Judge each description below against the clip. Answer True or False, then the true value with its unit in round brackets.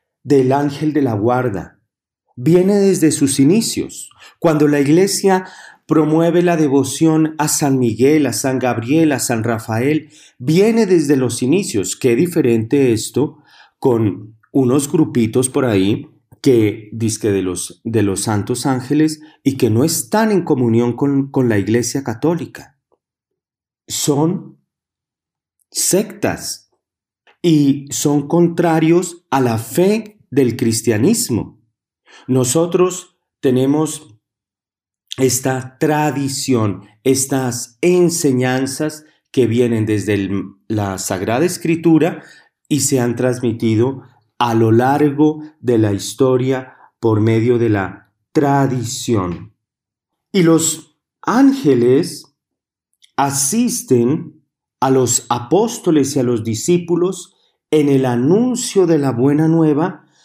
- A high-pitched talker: False (135 Hz)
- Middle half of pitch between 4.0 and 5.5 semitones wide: True (4.9 semitones)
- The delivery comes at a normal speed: False (110 wpm)